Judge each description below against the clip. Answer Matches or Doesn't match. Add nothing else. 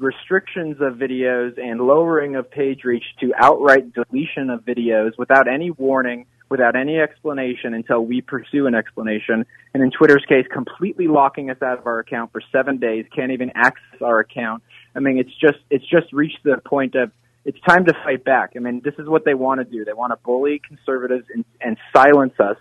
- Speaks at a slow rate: Doesn't match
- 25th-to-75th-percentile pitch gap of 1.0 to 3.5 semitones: Matches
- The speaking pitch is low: Matches